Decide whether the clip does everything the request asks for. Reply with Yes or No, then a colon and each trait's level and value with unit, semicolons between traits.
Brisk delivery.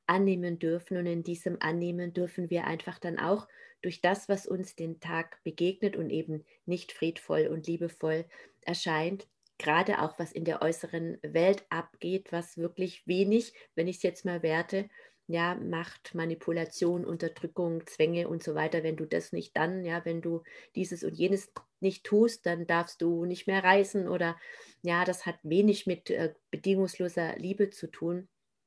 No: average, 165 wpm